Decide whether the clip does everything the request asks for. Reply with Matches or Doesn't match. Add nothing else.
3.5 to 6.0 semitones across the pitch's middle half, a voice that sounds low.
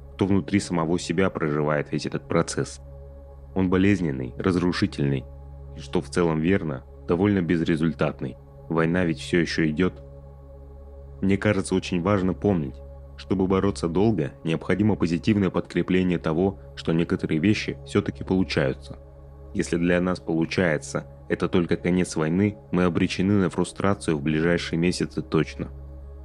Matches